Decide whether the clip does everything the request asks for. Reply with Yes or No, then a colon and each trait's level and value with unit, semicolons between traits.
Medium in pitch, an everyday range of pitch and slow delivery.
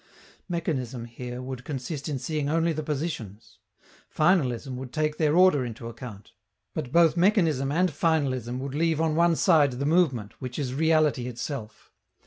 No: medium, 145 Hz; average, 4.3 semitones; average, 155 wpm